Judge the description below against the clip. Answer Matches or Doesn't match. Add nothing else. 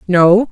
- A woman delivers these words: Matches